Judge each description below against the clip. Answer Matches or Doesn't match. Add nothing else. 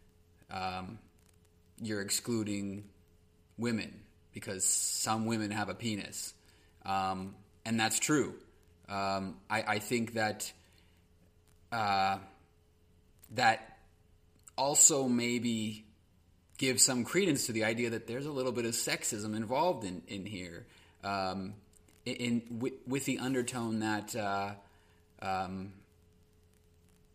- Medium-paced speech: Doesn't match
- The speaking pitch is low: Matches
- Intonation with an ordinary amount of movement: Matches